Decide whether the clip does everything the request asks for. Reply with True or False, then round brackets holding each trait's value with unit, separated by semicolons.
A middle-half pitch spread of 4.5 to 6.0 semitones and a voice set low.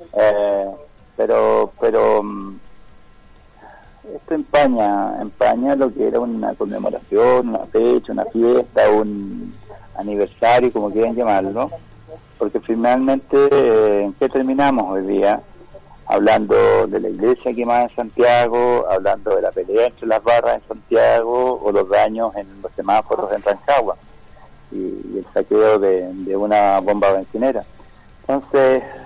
True (5.1 semitones; 120 Hz)